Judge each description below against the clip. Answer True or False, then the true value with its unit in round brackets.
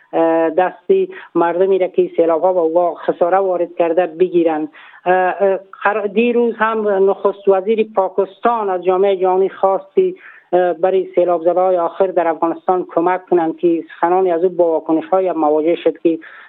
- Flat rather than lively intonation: True (2.2 semitones)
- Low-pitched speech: False (185 Hz)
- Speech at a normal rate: True (135 wpm)